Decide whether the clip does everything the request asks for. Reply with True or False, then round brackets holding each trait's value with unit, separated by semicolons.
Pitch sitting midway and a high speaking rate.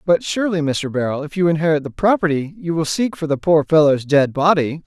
True (160 Hz; 220 wpm)